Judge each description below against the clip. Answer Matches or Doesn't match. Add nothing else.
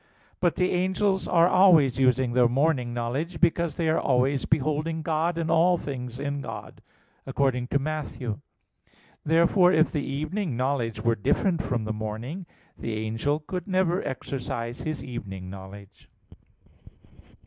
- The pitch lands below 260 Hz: Matches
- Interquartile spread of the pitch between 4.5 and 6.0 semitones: Matches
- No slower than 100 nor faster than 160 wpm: Matches